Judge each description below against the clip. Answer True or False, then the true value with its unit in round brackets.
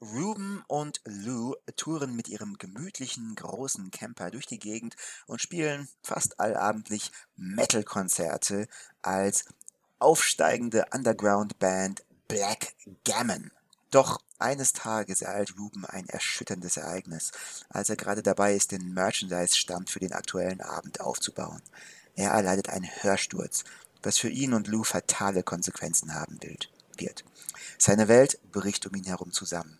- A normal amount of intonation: True (3.3 semitones)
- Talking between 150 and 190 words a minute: False (125 wpm)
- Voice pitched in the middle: False (105 Hz)